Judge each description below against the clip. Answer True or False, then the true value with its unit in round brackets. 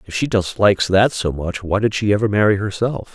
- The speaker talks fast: True (230 wpm)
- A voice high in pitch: False (100 Hz)